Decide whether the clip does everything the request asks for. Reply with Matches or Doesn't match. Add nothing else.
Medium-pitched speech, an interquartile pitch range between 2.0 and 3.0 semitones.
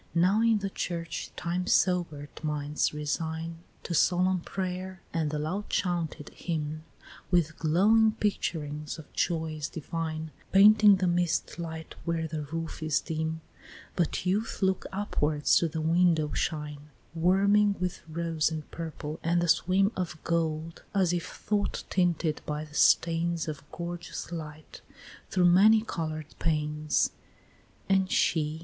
Matches